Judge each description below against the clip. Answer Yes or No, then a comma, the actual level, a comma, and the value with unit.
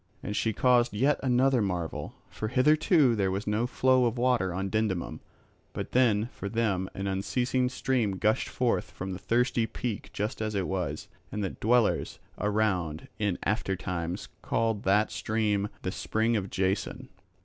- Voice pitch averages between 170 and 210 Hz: No, low, 110 Hz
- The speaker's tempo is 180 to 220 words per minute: No, average, 160 wpm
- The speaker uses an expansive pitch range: No, average, 4.1 semitones